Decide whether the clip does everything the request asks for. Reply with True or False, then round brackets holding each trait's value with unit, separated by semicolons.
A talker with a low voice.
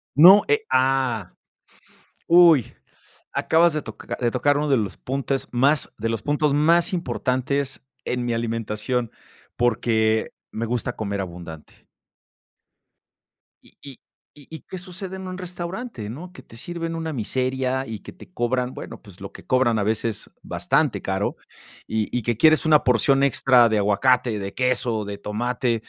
True (125 Hz)